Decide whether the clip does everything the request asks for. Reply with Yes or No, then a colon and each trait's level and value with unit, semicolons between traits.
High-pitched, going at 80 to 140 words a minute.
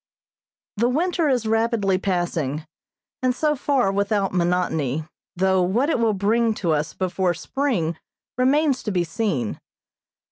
Yes: high, 200 Hz; slow, 135 wpm